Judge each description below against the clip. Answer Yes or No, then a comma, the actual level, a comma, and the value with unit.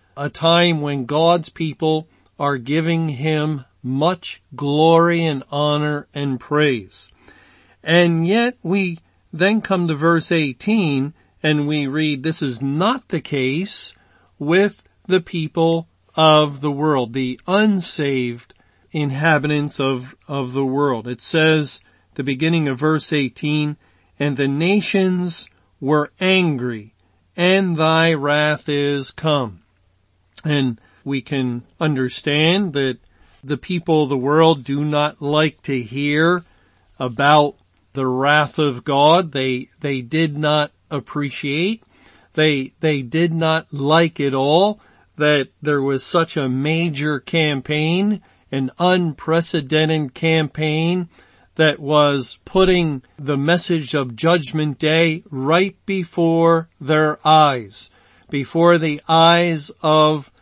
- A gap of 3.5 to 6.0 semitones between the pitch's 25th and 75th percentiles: No, average, 3.1 semitones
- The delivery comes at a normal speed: No, slow, 115 wpm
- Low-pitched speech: No, medium, 150 Hz